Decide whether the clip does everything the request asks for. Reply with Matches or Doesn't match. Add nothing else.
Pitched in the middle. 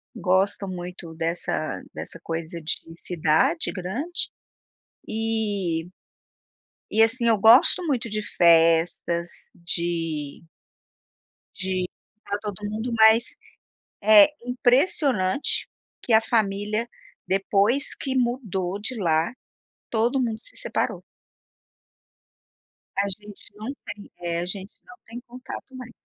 Doesn't match